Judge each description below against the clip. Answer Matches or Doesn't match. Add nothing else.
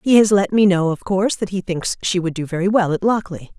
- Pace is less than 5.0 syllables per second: Doesn't match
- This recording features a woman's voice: Matches